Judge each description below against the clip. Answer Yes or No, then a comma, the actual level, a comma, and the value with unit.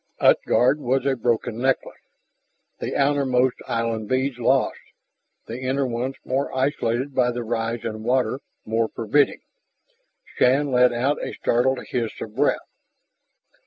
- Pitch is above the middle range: No, low, 125 Hz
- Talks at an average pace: No, slow, 130 wpm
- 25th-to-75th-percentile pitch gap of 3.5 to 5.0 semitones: No, narrow, 2.4 semitones